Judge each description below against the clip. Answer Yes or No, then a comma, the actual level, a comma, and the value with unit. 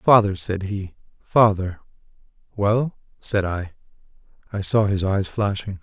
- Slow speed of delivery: Yes, slow, 125 wpm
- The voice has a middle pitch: No, low, 100 Hz